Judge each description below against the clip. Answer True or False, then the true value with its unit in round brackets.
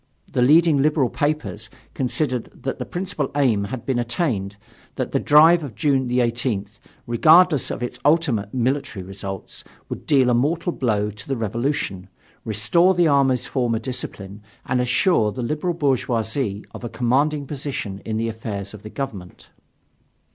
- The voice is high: False (125 Hz)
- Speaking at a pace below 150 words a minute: False (155 wpm)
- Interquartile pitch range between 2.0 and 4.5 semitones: False (4.9 semitones)